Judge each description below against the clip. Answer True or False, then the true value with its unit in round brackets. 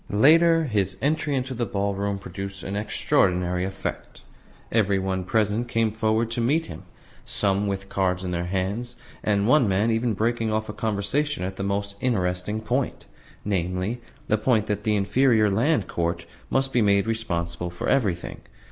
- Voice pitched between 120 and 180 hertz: False (105 Hz)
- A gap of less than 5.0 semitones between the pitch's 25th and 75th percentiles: True (3.4 semitones)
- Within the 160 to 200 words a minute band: True (165 wpm)